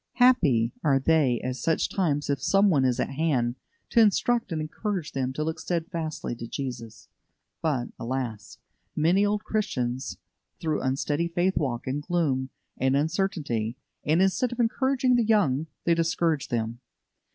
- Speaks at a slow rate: No, average, 150 wpm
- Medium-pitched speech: Yes, medium, 155 Hz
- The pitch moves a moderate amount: No, wide, 6.0 semitones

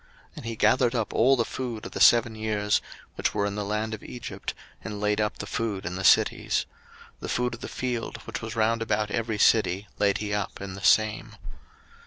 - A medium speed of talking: No, fast, 220 wpm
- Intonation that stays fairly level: Yes, narrow, 2.0 semitones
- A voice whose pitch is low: Yes, low, 110 Hz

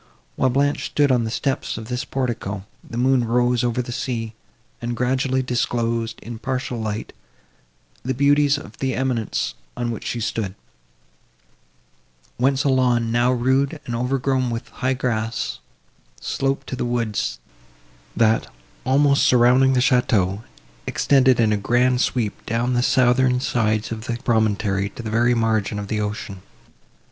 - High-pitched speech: No, low, 120 Hz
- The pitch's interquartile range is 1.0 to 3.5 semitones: Yes, narrow, 2.5 semitones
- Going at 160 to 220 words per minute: No, average, 150 wpm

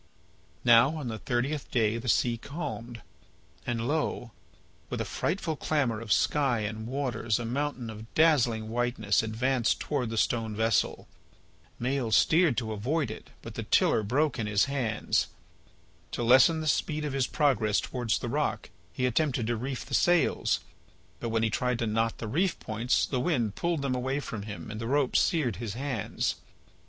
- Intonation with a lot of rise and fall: No, average, 4.0 semitones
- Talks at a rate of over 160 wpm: Yes, average, 175 wpm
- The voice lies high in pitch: No, low, 120 Hz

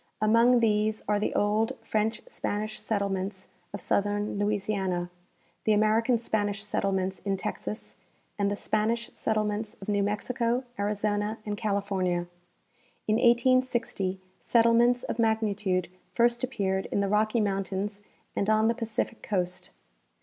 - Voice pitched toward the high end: Yes, high, 210 Hz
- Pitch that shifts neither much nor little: No, narrow, 2.1 semitones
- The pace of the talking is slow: Yes, slow, 130 wpm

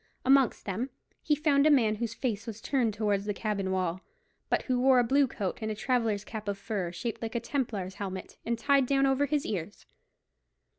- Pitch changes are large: No, average, 4.7 semitones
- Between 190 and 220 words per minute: Yes, fast, 205 wpm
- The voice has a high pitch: Yes, high, 225 Hz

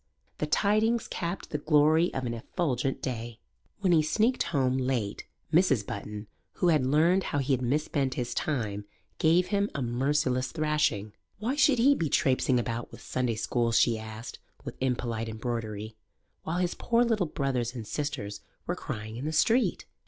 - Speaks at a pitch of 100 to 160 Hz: Yes, low, 135 Hz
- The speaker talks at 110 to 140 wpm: No, average, 165 wpm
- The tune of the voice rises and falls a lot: Yes, wide, 6.0 semitones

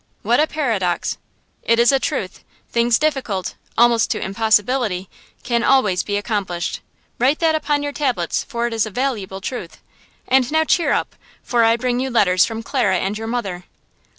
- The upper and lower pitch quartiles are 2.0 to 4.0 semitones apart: No, average, 4.6 semitones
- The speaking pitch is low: No, high, 235 Hz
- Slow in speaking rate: No, average, 165 wpm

